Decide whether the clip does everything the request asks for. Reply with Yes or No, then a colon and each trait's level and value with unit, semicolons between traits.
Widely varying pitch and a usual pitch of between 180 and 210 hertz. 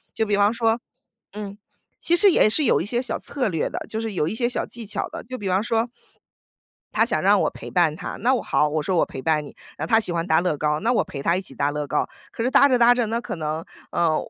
Yes: wide, 6.7 semitones; high, 200 Hz